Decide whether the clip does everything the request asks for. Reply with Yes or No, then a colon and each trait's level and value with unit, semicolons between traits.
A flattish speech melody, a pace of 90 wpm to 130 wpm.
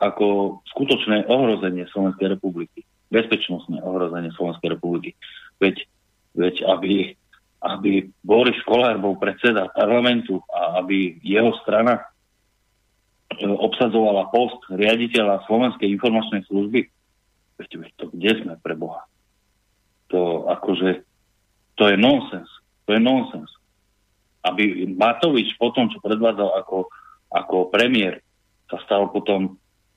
Yes: narrow, 2.2 semitones; slow, 110 wpm